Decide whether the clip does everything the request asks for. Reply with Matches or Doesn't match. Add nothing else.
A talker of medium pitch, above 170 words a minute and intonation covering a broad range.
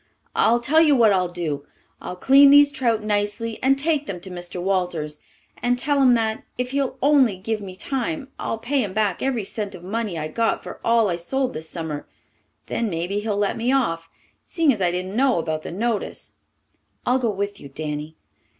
Doesn't match